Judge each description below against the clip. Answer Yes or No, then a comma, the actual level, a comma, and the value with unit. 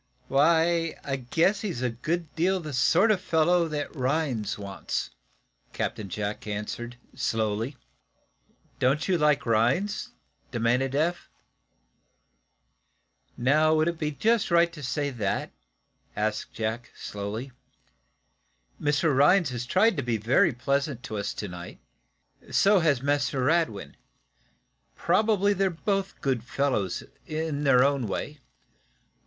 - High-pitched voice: No, medium, 140 Hz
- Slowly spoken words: Yes, slow, 125 wpm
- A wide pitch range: Yes, wide, 5.8 semitones